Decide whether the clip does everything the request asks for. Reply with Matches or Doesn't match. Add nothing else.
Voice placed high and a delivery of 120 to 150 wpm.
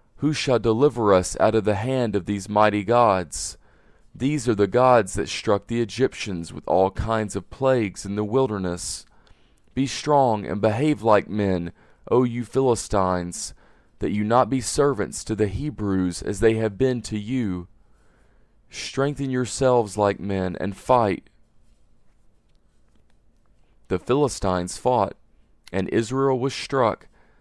Doesn't match